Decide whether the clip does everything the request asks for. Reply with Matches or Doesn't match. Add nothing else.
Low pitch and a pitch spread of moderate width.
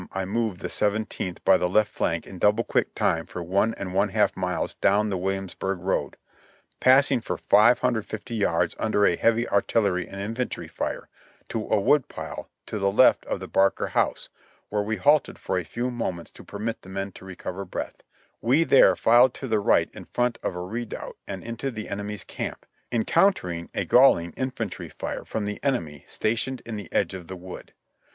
Matches